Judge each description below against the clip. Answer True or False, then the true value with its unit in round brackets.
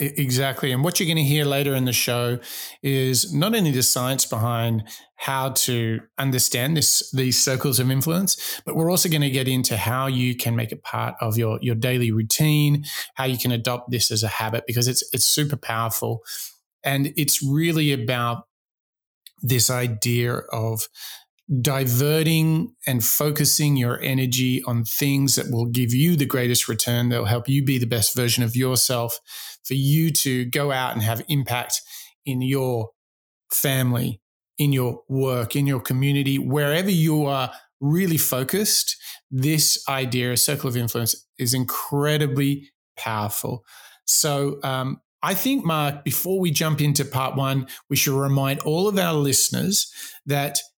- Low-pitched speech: True (130 Hz)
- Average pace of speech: True (160 wpm)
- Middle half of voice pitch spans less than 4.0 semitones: True (2.9 semitones)